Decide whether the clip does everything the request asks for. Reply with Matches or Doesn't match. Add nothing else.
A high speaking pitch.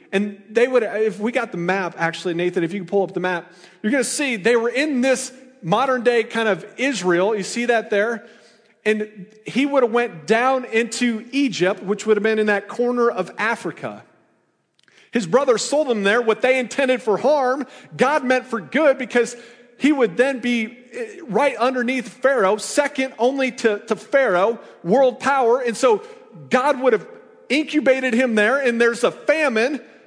Matches